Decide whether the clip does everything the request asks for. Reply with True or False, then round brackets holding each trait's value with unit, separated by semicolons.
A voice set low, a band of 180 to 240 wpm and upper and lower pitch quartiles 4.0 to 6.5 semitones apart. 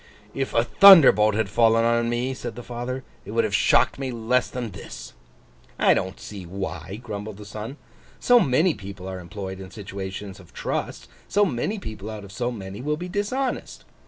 True (110 Hz; 190 wpm; 4.5 semitones)